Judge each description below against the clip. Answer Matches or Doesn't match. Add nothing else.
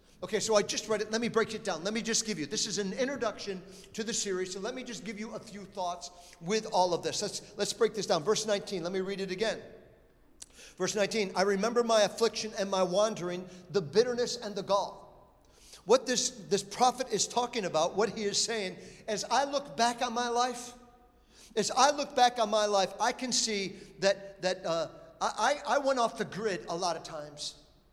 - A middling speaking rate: Doesn't match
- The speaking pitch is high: Matches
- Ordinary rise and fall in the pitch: Matches